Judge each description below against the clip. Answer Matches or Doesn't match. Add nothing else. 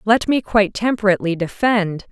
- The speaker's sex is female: Matches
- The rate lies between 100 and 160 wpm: Matches